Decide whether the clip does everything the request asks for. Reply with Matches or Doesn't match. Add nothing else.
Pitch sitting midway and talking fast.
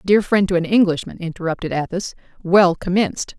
Doesn't match